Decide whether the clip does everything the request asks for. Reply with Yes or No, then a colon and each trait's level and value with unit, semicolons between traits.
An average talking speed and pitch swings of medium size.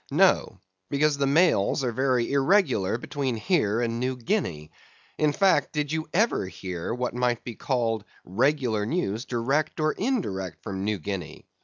No: average, 155 wpm; wide, 6.0 semitones